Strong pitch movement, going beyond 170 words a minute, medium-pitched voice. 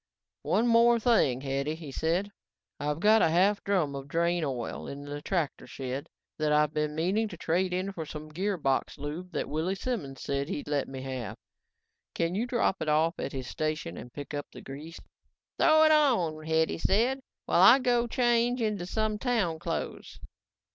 Yes: wide, 6.3 semitones; average, 180 wpm; medium, 165 Hz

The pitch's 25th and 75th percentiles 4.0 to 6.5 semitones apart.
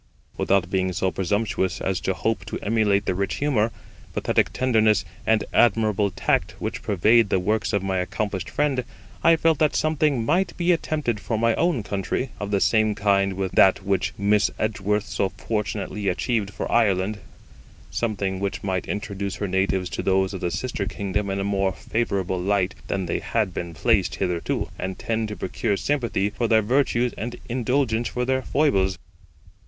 No: average, 3.3 semitones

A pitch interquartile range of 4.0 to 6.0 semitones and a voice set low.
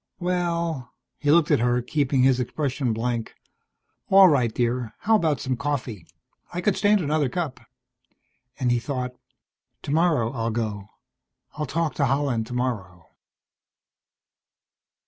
Yes: average, 4.7 semitones; low, 130 Hz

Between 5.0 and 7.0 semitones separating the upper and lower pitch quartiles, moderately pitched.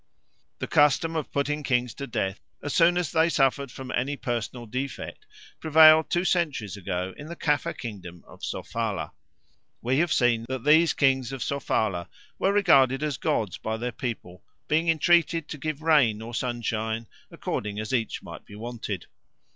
No: wide, 5.4 semitones; low, 130 Hz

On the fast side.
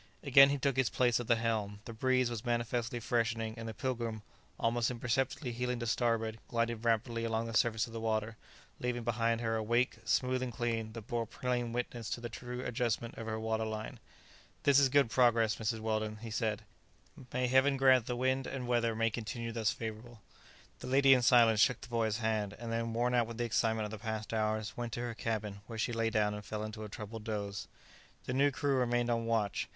Yes: fast, 215 wpm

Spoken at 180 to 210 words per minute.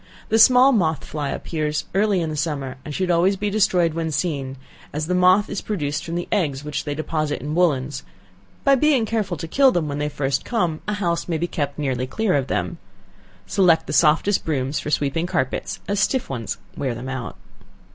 Yes: fast, 205 wpm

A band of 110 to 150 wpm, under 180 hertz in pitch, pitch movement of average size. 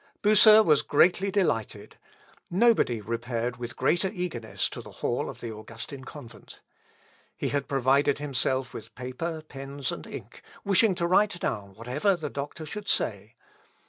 No: average, 145 wpm; medium, 140 Hz; wide, 6.9 semitones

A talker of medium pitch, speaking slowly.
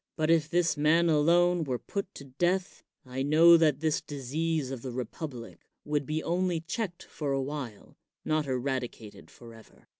No: medium, 150 Hz; average, 160 wpm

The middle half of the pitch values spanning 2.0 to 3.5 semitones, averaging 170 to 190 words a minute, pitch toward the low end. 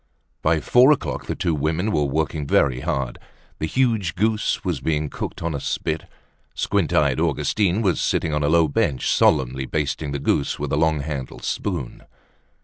Yes: average, 3.2 semitones; average, 175 wpm; very low, 80 Hz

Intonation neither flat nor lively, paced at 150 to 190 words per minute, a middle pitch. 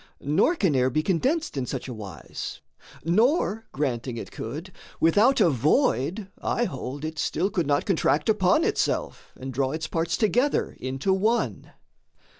No: wide, 7.9 semitones; average, 155 wpm; medium, 160 Hz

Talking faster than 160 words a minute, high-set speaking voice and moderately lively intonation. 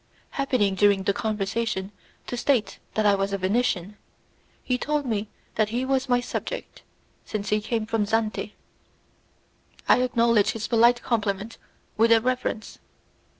No: average, 145 wpm; high, 220 Hz; average, 3.1 semitones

